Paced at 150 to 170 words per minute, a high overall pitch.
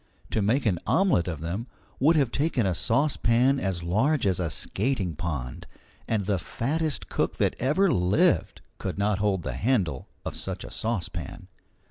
No: average, 165 wpm; low, 105 Hz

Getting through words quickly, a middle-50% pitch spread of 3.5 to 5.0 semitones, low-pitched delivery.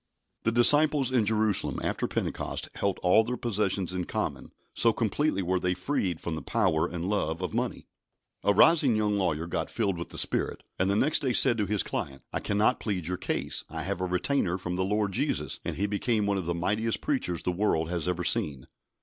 Yes: fast, 210 wpm; average, 3.8 semitones; low, 100 Hz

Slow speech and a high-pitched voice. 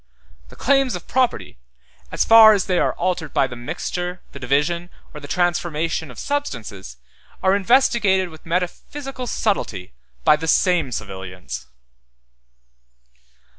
No: slow, 130 wpm; medium, 175 Hz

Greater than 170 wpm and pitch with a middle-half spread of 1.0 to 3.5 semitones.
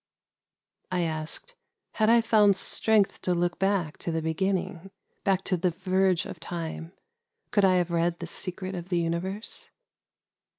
Yes: average, 180 wpm; narrow, 2.4 semitones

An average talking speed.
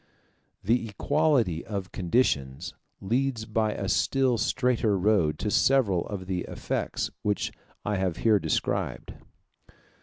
No: slow, 120 wpm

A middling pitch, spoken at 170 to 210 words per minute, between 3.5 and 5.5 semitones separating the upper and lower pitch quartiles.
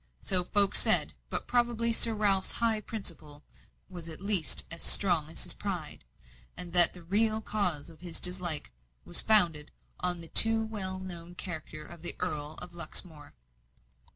No: medium, 180 Hz; average, 160 wpm; average, 4.1 semitones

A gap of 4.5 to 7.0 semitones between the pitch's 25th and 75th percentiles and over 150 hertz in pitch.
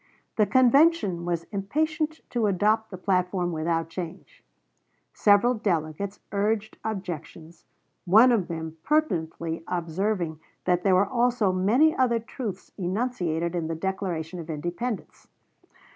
Yes: average, 4.9 semitones; high, 190 Hz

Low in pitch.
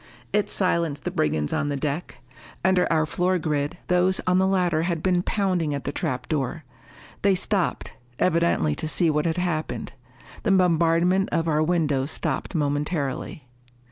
No: medium, 165 Hz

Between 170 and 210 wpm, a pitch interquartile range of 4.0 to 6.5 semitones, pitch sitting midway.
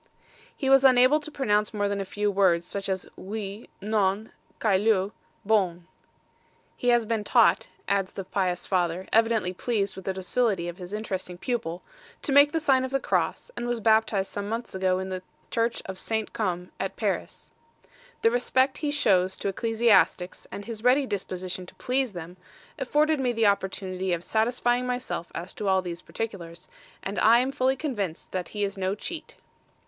No: average, 180 wpm; average, 4.4 semitones; high, 205 Hz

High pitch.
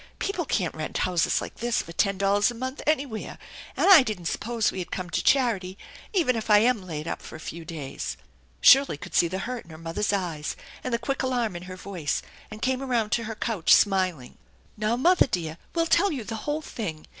Yes: high, 210 Hz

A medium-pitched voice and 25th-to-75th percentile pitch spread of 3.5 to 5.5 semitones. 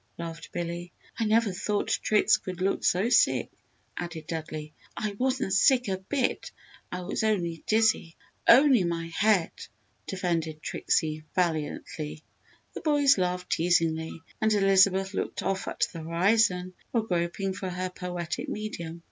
Yes: medium, 180 Hz; average, 3.9 semitones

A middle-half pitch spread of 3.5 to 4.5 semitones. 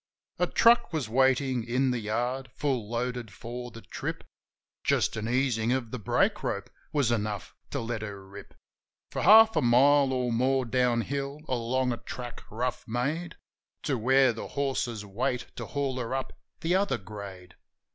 No: average, 2.8 semitones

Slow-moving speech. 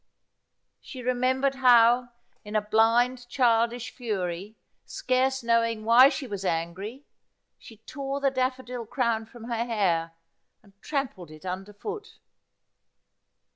Yes: slow, 130 wpm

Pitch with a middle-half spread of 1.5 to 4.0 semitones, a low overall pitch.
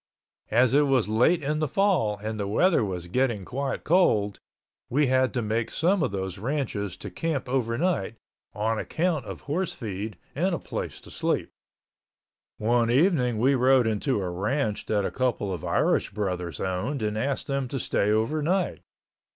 No: average, 5.3 semitones; low, 120 Hz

